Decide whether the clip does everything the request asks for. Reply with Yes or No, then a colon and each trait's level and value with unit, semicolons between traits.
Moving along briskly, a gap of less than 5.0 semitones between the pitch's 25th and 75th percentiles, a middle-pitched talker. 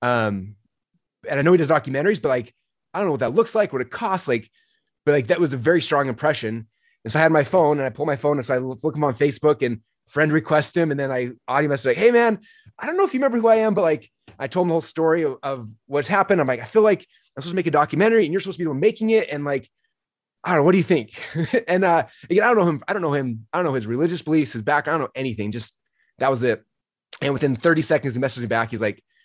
No: fast, 300 wpm; wide, 5.4 semitones; medium, 150 Hz